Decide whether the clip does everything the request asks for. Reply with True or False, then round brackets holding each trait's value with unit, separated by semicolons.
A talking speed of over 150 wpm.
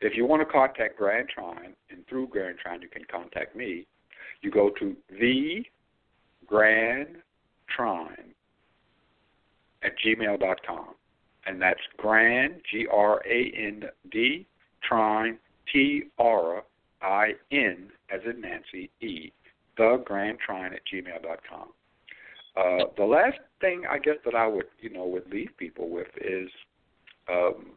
False (135 wpm)